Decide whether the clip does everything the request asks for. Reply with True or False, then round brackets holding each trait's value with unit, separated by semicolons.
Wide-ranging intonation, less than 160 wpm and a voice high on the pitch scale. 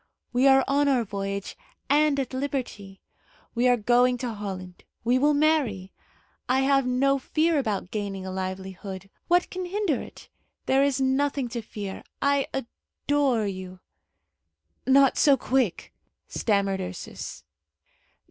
True (5.8 semitones; 135 wpm; 250 Hz)